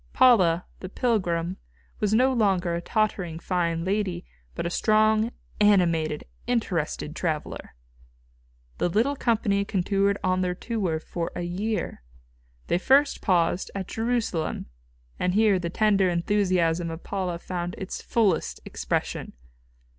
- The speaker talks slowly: Yes, slow, 125 wpm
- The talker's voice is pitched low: No, medium, 185 Hz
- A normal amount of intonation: Yes, average, 3.8 semitones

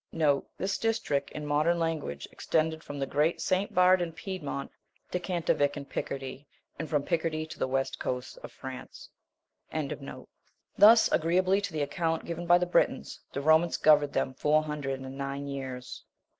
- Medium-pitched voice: Yes, medium, 155 Hz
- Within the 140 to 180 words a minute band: Yes, average, 170 wpm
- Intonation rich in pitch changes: No, average, 3.7 semitones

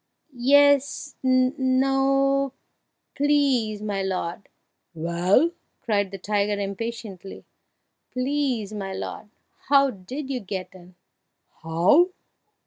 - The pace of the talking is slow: Yes, slow, 95 wpm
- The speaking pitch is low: No, high, 230 Hz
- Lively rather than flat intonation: Yes, wide, 5.8 semitones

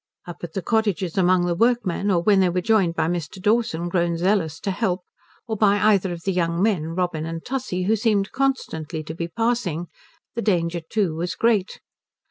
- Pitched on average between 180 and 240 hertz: Yes, medium, 185 Hz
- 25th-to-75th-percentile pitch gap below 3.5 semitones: No, average, 4.0 semitones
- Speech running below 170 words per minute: No, average, 195 wpm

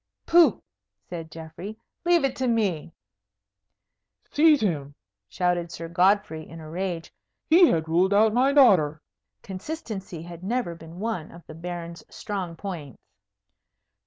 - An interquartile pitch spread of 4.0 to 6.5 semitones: Yes, average, 5.0 semitones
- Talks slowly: Yes, slow, 130 wpm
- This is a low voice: No, medium, 180 Hz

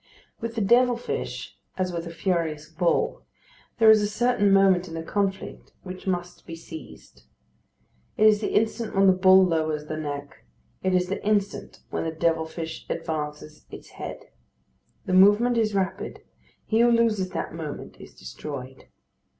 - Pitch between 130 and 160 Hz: No, medium, 185 Hz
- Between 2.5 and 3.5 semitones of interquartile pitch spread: No, average, 4.3 semitones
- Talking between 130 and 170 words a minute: Yes, average, 165 wpm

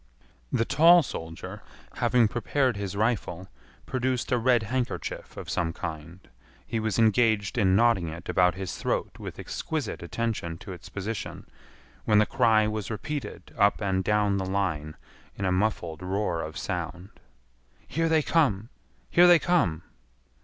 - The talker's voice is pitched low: Yes, low, 105 Hz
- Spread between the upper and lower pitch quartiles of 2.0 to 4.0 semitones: No, average, 4.6 semitones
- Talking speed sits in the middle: Yes, average, 150 wpm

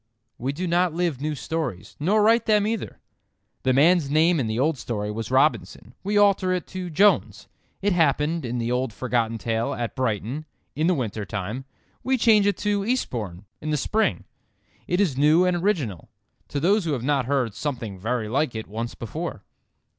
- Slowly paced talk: No, average, 180 wpm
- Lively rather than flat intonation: Yes, wide, 7.5 semitones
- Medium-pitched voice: Yes, medium, 145 Hz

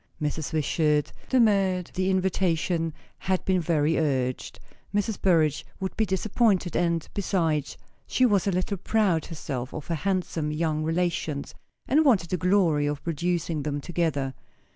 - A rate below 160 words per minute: Yes, average, 140 wpm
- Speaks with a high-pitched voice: No, medium, 170 Hz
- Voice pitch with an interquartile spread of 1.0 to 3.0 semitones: No, average, 3.7 semitones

